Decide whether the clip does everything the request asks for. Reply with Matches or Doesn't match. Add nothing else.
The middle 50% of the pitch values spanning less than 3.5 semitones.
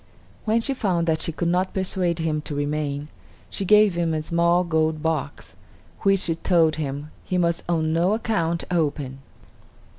Matches